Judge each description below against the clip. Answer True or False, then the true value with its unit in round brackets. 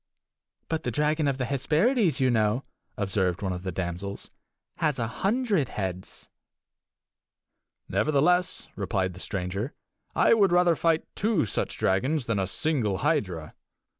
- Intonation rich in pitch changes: True (8.8 semitones)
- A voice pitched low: True (130 Hz)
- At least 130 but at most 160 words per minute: True (135 wpm)